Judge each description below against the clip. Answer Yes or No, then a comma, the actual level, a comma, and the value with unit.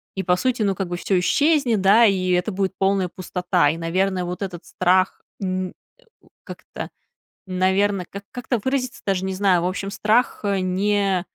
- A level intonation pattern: Yes, narrow, 2.0 semitones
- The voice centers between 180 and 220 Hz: Yes, high, 190 Hz